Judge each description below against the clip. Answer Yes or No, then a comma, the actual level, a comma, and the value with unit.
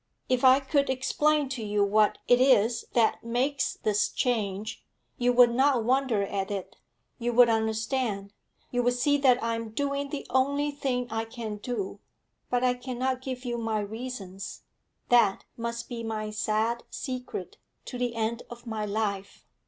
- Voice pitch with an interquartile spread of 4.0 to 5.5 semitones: No, average, 3.0 semitones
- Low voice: No, high, 240 Hz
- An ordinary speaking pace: Yes, average, 165 wpm